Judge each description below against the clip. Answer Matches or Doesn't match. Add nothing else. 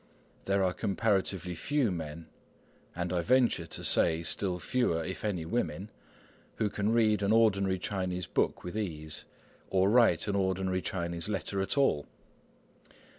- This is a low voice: Matches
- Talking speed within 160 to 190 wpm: Doesn't match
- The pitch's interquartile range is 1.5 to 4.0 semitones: Matches